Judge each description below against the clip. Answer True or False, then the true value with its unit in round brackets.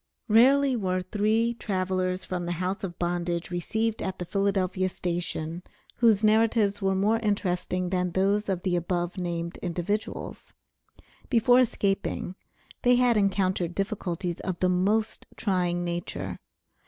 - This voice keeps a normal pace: False (130 wpm)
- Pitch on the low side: False (190 Hz)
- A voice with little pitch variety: False (3.1 semitones)